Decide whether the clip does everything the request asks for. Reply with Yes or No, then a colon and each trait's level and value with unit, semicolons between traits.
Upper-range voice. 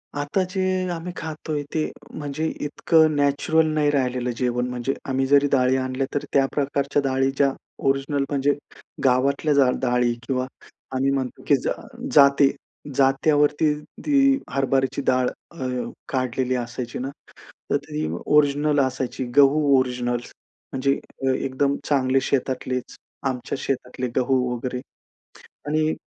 No: low, 135 Hz